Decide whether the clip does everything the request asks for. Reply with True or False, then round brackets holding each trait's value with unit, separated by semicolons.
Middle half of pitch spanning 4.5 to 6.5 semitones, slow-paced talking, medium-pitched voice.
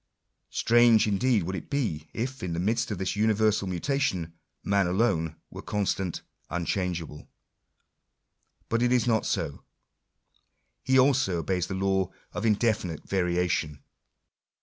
False (4.8 semitones; 125 wpm; 100 Hz)